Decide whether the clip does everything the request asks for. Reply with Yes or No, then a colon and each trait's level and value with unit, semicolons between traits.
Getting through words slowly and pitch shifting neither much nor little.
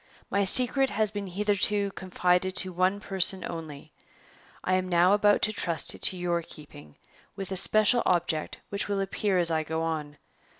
No: average, 175 wpm; average, 3.1 semitones